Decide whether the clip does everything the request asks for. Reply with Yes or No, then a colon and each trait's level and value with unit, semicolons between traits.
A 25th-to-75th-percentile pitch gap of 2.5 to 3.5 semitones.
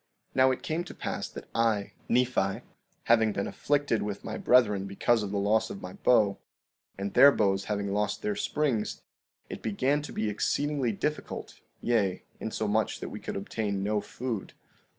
No: average, 3.9 semitones